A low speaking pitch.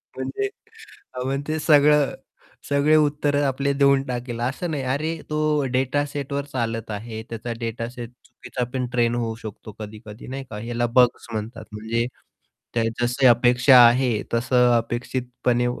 Yes: low, 125 Hz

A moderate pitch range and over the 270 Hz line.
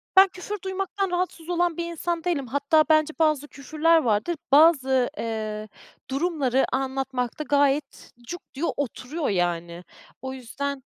Yes: average, 4.5 semitones; very high, 285 Hz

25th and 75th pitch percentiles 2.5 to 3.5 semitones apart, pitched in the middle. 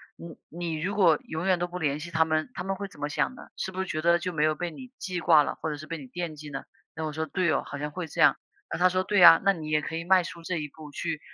Yes: average, 2.8 semitones; medium, 165 Hz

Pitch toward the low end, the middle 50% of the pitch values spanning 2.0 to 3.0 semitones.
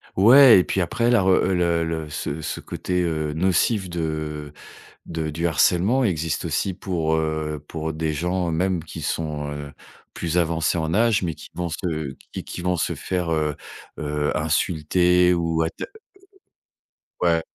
Yes: very low, 80 Hz; narrow, 2.5 semitones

